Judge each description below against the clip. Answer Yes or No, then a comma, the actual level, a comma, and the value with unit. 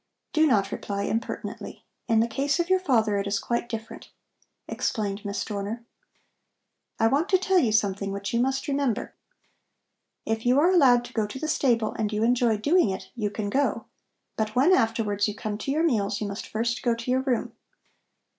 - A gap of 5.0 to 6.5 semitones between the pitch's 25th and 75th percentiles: No, average, 4.3 semitones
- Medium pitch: No, high, 230 Hz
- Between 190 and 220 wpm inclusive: Yes, average, 195 wpm